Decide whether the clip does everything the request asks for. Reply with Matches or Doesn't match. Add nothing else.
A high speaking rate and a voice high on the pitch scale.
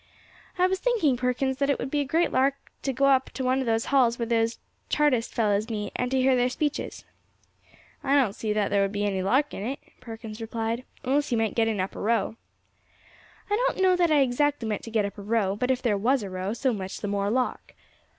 Matches